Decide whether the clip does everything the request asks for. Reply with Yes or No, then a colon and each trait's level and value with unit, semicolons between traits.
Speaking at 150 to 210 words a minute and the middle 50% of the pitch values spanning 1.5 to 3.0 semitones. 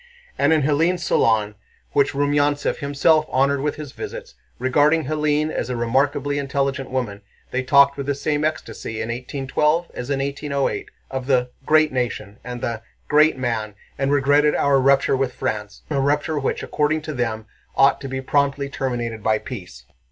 Yes: average, 165 wpm; average, 2.7 semitones